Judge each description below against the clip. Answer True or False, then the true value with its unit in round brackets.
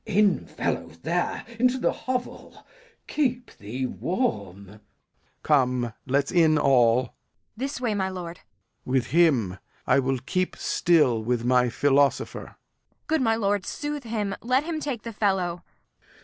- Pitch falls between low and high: True (170 Hz)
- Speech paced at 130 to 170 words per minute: True (150 wpm)